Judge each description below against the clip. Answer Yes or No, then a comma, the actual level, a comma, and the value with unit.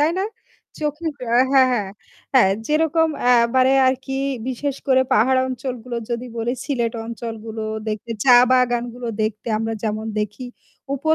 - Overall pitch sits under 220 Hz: No, high, 245 Hz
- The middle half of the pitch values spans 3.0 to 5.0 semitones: No, narrow, 2.6 semitones